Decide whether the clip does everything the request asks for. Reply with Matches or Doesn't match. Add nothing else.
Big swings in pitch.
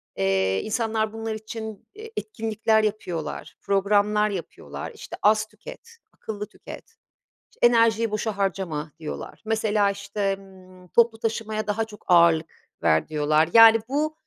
Doesn't match